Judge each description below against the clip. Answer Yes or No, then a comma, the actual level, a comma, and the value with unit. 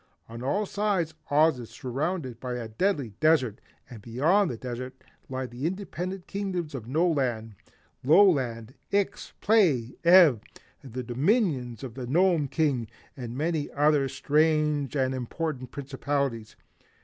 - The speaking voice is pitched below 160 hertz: Yes, medium, 140 Hz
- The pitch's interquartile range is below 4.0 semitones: No, average, 5.3 semitones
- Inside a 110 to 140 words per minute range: Yes, slow, 135 wpm